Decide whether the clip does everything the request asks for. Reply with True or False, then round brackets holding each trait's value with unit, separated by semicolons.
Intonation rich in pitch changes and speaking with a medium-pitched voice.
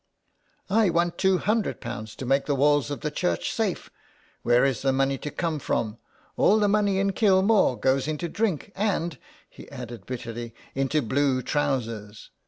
True (7.0 semitones; 145 Hz)